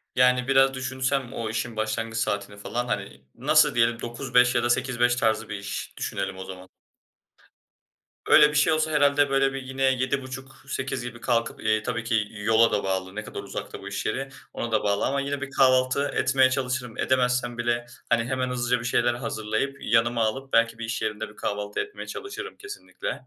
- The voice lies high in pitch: No, low, 120 Hz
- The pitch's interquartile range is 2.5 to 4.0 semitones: Yes, average, 2.9 semitones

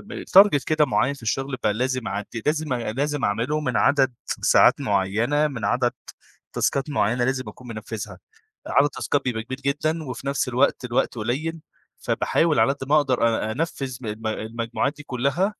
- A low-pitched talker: Yes, low, 130 Hz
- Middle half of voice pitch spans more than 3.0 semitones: Yes, average, 4.0 semitones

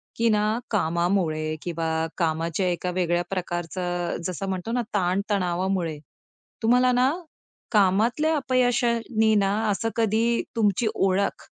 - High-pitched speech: Yes, high, 195 Hz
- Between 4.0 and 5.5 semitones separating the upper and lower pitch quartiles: Yes, average, 4.4 semitones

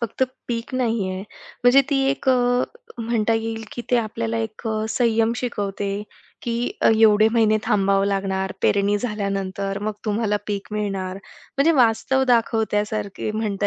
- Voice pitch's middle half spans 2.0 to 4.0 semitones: Yes, average, 2.7 semitones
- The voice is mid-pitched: No, high, 215 Hz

